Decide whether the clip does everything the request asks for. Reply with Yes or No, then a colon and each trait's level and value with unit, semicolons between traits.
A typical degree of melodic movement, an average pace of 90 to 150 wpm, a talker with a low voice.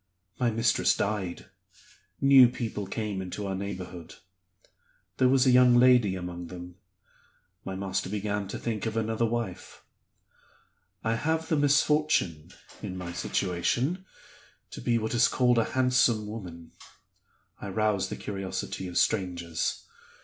Yes: average, 4.8 semitones; slow, 135 wpm; low, 105 Hz